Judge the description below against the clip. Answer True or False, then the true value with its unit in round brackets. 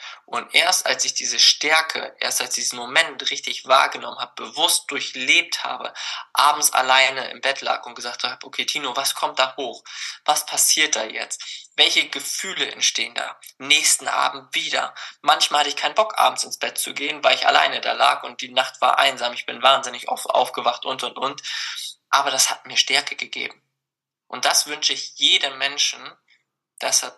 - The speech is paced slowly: False (185 wpm)